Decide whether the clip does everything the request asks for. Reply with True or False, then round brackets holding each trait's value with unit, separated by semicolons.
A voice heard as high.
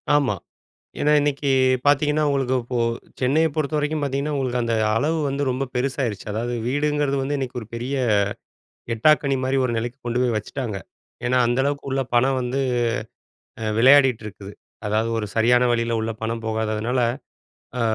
False (130 Hz)